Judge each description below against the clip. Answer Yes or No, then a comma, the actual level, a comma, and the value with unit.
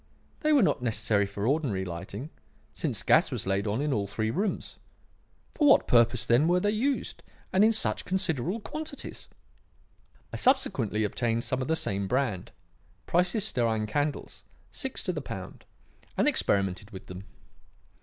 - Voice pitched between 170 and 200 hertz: No, low, 125 Hz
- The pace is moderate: Yes, average, 155 wpm